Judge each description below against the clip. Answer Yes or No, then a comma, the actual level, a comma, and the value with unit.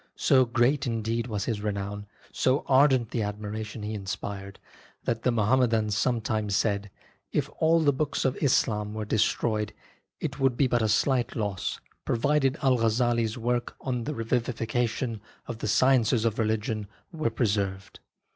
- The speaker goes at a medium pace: Yes, average, 155 wpm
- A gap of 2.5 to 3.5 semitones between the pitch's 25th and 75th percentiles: Yes, average, 3.0 semitones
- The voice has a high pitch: No, low, 115 Hz